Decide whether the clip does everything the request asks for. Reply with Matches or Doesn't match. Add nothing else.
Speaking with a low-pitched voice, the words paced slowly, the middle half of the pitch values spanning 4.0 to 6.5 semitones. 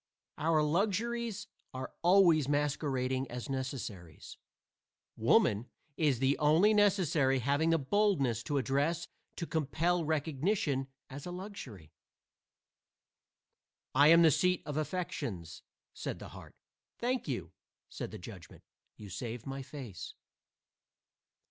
Doesn't match